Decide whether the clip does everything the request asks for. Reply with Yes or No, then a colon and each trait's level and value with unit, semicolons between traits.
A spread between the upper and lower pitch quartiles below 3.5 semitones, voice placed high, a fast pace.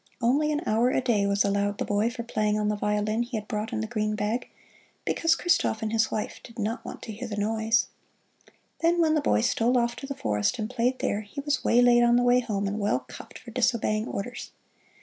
Yes: average, 2.7 semitones; high, 225 Hz; fast, 230 wpm